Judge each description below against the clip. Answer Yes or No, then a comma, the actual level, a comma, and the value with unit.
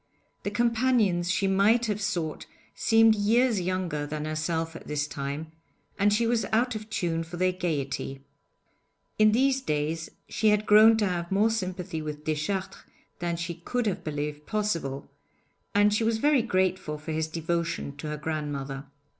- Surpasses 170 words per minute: No, average, 165 wpm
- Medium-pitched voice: Yes, medium, 180 Hz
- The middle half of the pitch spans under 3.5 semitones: No, wide, 5.6 semitones